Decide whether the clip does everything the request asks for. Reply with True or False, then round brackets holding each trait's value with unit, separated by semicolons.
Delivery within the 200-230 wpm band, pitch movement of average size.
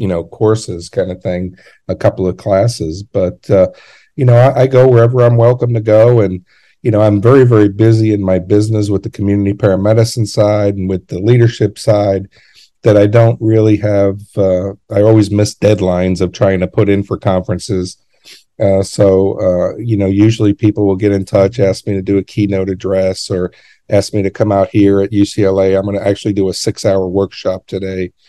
False (205 wpm; 2.2 semitones)